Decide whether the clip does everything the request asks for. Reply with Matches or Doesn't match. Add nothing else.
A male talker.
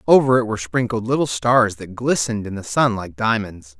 Matches